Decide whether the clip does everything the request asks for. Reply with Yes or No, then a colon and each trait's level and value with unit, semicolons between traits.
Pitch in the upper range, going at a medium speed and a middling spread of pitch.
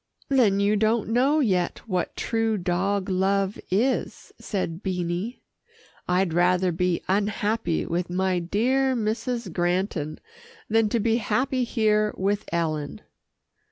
No: high, 200 Hz; slow, 125 wpm; average, 3.9 semitones